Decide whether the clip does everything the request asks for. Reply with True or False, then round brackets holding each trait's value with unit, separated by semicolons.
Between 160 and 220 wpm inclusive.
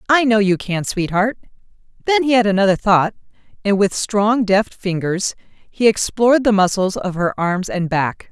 True (175 wpm)